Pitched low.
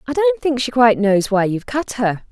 No: high, 245 Hz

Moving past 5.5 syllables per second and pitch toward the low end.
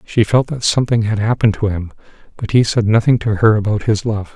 Yes: 6.0 syllables/s; low, 110 Hz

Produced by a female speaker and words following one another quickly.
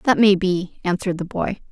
Yes: female; fast, 210 wpm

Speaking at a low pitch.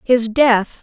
No: high, 235 Hz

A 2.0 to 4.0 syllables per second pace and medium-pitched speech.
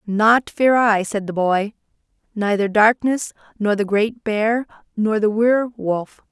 No: 3.9 syllables/s; high, 215 Hz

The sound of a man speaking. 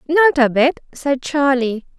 No: female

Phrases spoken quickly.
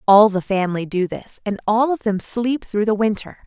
Yes: fast, 225 wpm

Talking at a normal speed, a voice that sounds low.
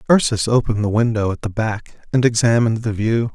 Yes: average, 195 wpm; low, 110 Hz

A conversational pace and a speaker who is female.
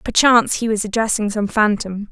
Yes: average, 170 wpm; female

